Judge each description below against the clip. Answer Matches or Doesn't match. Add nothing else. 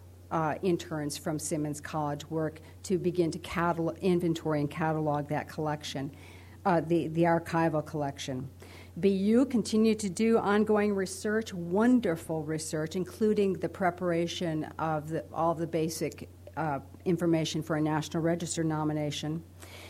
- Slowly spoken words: Matches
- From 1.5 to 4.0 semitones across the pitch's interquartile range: Matches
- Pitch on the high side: Doesn't match